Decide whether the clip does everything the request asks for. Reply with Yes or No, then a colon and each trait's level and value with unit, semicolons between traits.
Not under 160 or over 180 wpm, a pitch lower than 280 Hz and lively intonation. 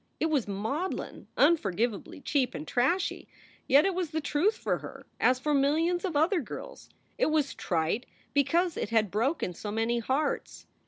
No: average, 165 wpm; very high, 285 Hz; wide, 6.2 semitones